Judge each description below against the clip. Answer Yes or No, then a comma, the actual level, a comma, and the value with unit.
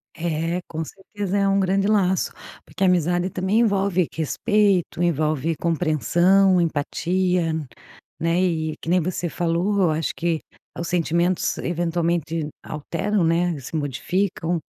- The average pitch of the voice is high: No, medium, 175 Hz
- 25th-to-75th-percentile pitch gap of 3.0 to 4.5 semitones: No, narrow, 2.5 semitones